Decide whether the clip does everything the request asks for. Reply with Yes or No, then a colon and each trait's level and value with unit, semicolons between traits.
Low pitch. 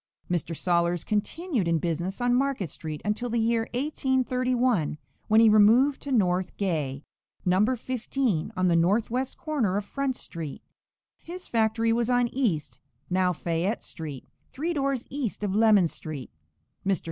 No: high, 215 Hz